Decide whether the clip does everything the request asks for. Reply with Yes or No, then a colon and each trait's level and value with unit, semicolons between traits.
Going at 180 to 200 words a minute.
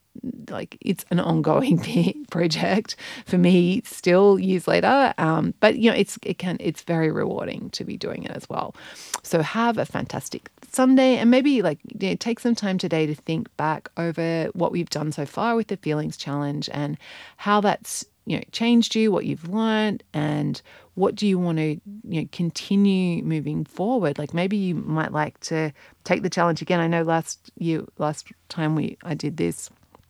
Yes: average, 185 wpm